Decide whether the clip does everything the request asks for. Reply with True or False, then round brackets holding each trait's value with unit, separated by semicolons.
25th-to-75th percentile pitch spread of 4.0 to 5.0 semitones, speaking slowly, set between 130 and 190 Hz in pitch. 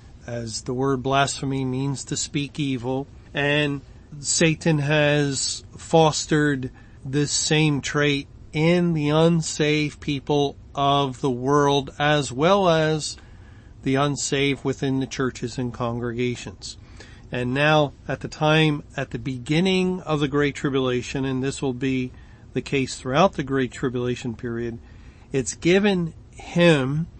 False (3.2 semitones; 130 wpm; 135 Hz)